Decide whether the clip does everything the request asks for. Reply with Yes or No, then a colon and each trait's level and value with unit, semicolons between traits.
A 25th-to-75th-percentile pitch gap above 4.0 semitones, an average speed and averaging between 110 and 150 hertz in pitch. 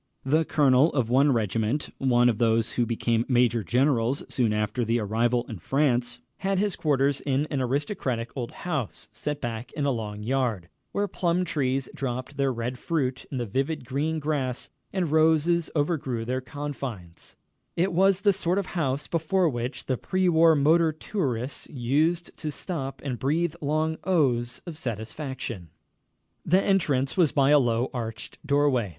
Yes: average, 4.6 semitones; average, 165 wpm; low, 135 Hz